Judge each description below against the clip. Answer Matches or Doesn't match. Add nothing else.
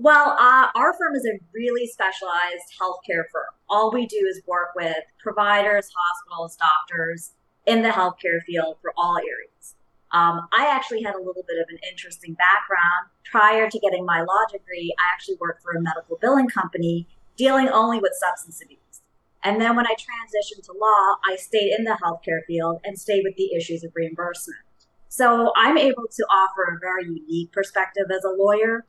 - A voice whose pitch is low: Doesn't match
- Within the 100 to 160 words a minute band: Doesn't match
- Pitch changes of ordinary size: Matches